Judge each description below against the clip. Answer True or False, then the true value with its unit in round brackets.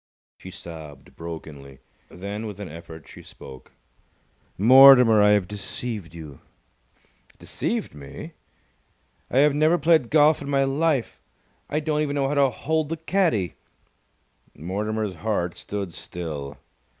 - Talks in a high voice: False (105 Hz)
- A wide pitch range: True (9.0 semitones)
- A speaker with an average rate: False (130 wpm)